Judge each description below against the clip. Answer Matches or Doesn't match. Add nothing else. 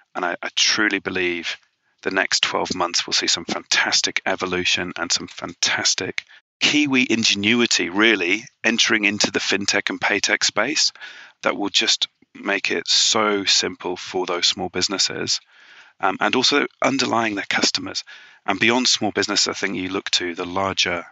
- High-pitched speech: Doesn't match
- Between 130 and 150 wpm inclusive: Doesn't match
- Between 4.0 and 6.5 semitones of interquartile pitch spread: Matches